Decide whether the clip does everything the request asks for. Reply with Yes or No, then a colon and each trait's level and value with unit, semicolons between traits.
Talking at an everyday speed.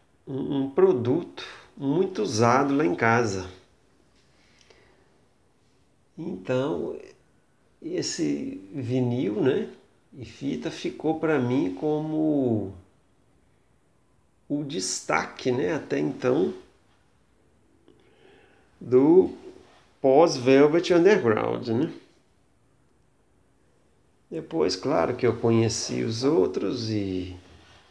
No: slow, 75 wpm